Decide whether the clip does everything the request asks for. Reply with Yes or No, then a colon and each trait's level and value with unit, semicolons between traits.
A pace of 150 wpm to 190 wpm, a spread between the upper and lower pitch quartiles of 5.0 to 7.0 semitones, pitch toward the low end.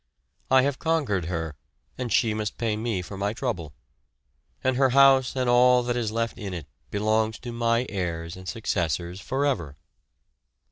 Yes: average, 160 wpm; average, 5.3 semitones; low, 110 Hz